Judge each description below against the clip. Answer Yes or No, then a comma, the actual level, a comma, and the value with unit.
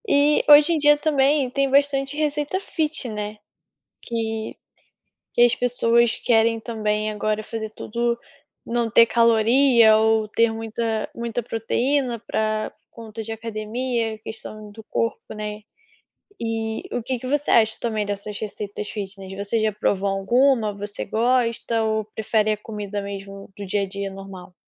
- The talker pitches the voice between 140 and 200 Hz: No, high, 225 Hz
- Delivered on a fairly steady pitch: Yes, narrow, 2.3 semitones